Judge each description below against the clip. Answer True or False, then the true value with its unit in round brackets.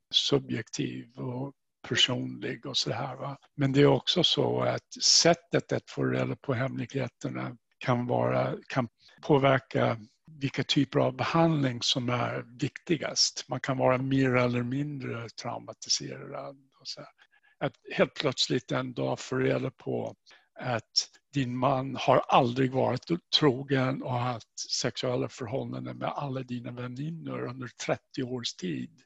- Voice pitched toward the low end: True (130 Hz)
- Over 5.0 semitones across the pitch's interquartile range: False (2.4 semitones)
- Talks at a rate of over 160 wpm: False (140 wpm)